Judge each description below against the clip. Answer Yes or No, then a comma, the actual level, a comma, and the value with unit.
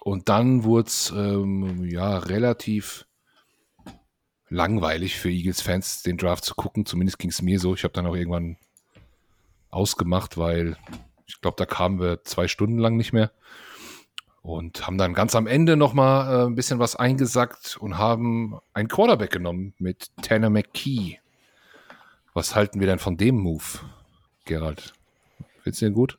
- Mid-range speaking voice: No, very low, 95 Hz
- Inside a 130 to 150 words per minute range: No, average, 160 wpm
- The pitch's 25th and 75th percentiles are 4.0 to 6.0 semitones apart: Yes, average, 4.4 semitones